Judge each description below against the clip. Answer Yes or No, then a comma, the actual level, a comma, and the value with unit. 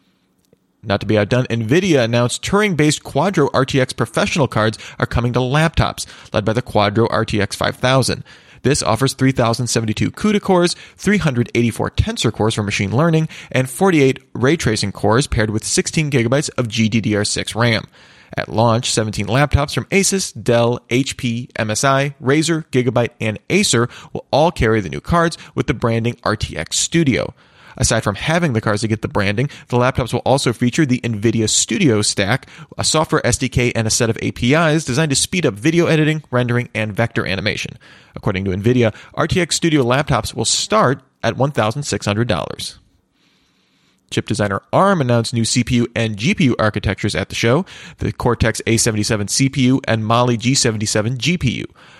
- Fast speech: No, average, 155 wpm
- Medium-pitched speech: No, low, 120 Hz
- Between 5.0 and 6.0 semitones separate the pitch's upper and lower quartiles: No, average, 4.6 semitones